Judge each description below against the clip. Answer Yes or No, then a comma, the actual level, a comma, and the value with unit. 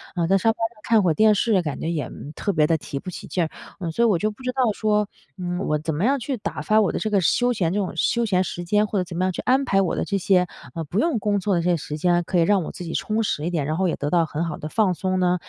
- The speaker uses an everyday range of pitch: Yes, average, 4.0 semitones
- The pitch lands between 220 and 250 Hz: No, medium, 185 Hz